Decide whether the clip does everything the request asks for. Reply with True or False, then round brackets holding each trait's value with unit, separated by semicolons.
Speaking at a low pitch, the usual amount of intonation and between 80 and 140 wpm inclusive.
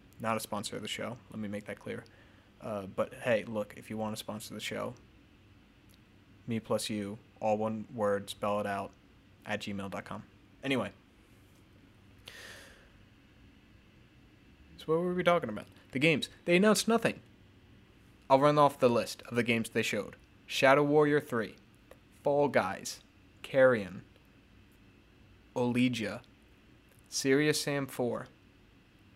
True (105 Hz; 3.8 semitones; 135 wpm)